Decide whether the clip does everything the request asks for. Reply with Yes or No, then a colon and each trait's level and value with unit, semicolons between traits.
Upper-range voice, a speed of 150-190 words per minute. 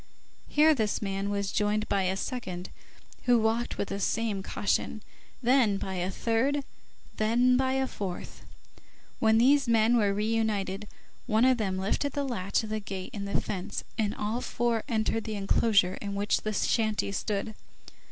Yes: high, 215 Hz; average, 170 wpm